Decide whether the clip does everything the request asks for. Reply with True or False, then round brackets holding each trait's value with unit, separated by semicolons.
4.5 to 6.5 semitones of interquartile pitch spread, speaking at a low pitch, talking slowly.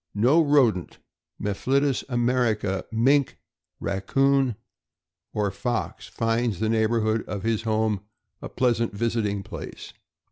False (3.1 semitones; 115 Hz; 105 wpm)